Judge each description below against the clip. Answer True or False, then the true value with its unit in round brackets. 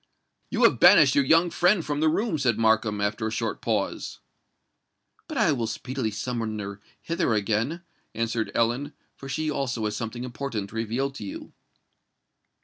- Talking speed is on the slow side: False (165 wpm)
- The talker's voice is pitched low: True (120 Hz)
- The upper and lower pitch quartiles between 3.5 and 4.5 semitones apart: False (5.3 semitones)